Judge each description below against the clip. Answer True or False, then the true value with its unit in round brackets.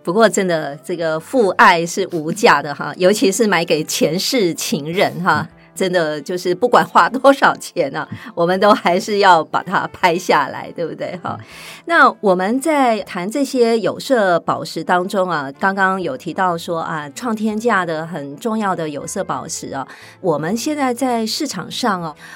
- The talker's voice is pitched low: False (185 Hz)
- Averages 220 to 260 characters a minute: True (240 characters per minute)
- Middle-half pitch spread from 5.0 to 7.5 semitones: True (5.3 semitones)